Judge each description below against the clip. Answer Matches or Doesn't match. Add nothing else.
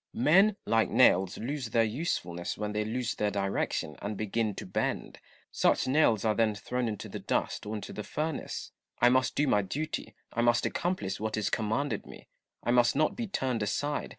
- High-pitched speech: Doesn't match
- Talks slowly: Doesn't match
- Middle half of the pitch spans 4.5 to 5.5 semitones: Doesn't match